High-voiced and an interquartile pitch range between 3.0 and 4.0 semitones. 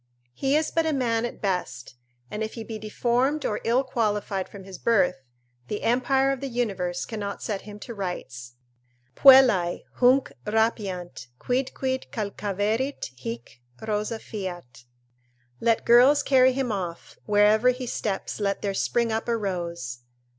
No: high, 215 Hz; average, 4.6 semitones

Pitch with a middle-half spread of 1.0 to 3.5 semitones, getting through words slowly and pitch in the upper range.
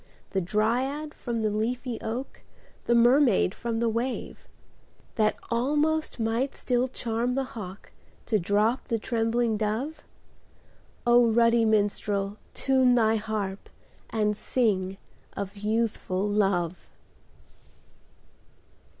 Yes: average, 2.8 semitones; slow, 105 wpm; high, 225 Hz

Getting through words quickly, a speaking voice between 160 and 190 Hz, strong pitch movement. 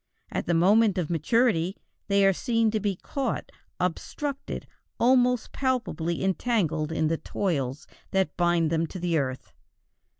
No: slow, 135 wpm; medium, 185 Hz; wide, 5.7 semitones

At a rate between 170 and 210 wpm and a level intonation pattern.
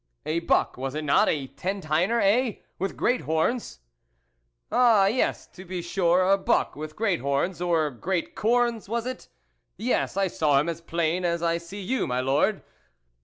No: average, 185 wpm; average, 4.8 semitones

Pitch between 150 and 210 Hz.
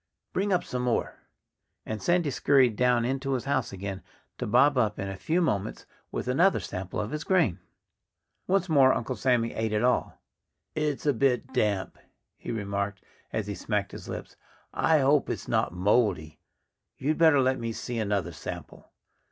No: low, 125 Hz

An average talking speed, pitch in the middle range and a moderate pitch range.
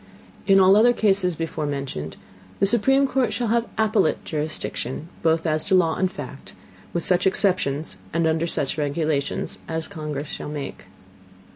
Yes: average, 165 wpm; medium, 165 Hz; average, 4.6 semitones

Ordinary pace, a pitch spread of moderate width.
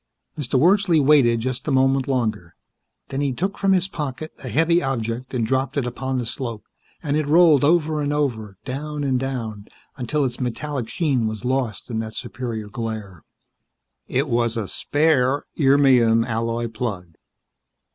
Yes: average, 160 wpm; average, 4.1 semitones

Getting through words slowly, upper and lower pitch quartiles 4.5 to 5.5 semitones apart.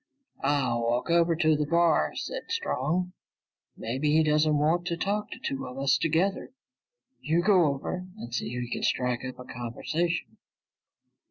No: average, 165 wpm; average, 5.0 semitones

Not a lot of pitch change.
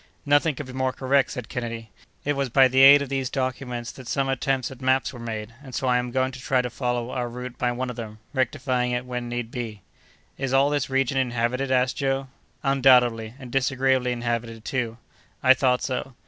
Yes: narrow, 1.7 semitones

